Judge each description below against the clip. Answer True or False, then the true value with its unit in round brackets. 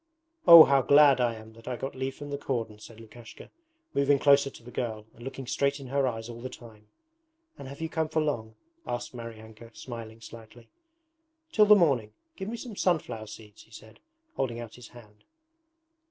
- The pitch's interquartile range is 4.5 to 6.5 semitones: False (3.8 semitones)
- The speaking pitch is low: True (120 Hz)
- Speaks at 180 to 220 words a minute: True (195 wpm)